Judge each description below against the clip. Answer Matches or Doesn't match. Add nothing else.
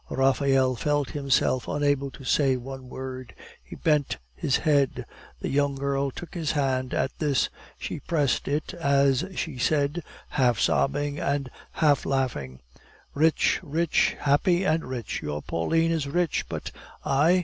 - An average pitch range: Doesn't match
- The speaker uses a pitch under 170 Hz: Matches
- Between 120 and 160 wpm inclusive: Matches